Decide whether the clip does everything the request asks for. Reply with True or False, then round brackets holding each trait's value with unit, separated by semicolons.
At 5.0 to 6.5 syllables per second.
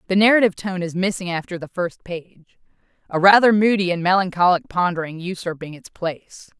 True (5.7 syllables/s)